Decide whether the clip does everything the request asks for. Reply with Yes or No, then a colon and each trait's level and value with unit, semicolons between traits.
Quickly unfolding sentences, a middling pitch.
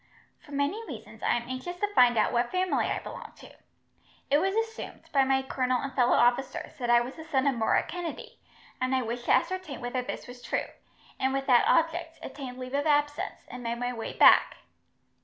No: fast, 210 wpm; very high, 265 Hz